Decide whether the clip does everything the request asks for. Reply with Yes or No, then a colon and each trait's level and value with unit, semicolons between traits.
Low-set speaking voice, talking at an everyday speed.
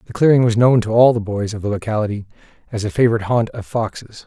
No: low, 110 Hz; fast, 240 wpm